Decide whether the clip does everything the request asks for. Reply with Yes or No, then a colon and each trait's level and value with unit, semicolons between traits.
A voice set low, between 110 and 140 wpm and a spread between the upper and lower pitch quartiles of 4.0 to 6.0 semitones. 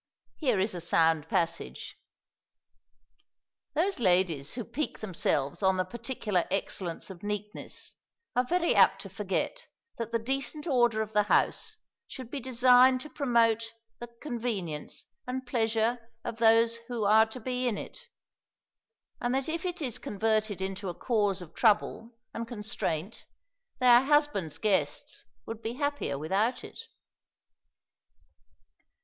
No: high, 225 Hz; slow, 135 wpm; average, 4.5 semitones